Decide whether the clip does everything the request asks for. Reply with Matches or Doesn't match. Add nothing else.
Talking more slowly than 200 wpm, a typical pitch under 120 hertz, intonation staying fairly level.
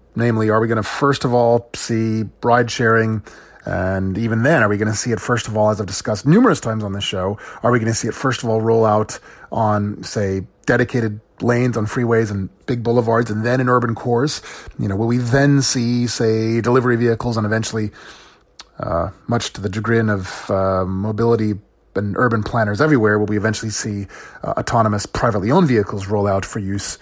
Doesn't match